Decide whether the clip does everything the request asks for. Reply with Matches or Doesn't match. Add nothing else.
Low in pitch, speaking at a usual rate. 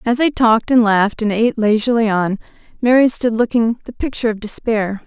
Doesn't match